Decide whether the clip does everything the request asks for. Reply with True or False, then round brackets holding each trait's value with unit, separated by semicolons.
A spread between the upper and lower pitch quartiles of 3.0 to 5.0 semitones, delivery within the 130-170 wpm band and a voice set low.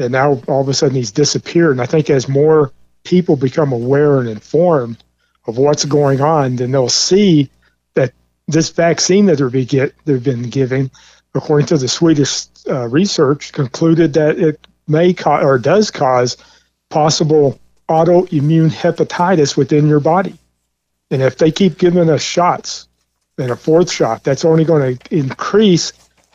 False (3.8 semitones; 155 wpm; 145 Hz)